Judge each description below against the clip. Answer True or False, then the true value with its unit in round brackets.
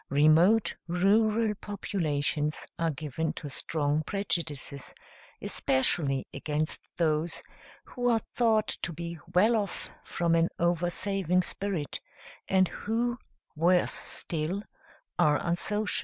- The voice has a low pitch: False (170 Hz)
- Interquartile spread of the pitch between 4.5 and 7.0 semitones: True (4.8 semitones)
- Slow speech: True (105 wpm)